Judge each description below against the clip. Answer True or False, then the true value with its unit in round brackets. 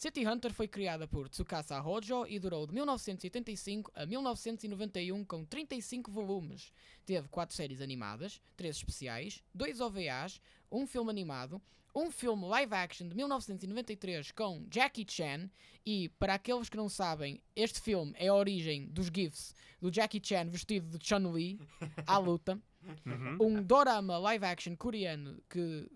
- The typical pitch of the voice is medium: False (195 Hz)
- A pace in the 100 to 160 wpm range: True (145 wpm)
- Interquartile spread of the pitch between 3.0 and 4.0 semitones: False (4.5 semitones)